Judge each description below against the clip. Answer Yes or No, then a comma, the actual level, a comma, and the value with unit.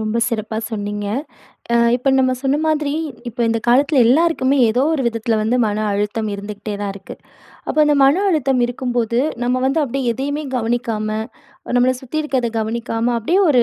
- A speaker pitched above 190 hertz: Yes, high, 240 Hz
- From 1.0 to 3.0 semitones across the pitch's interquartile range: No, average, 3.6 semitones